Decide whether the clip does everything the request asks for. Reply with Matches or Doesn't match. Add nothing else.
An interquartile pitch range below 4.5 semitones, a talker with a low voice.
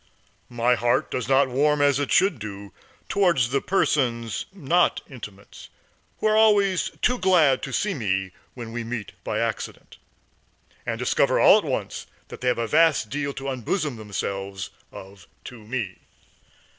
Doesn't match